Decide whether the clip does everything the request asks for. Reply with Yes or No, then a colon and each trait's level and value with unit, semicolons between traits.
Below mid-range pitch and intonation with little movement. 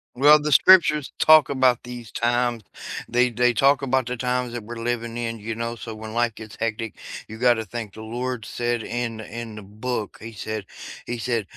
Yes: low, 120 Hz; narrow, 2.0 semitones